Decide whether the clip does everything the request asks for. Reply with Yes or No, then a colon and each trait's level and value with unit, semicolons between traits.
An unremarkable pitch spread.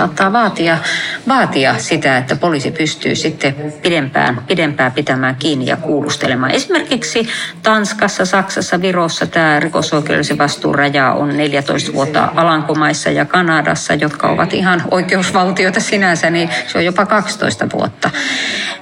Yes: average, 4.4 semitones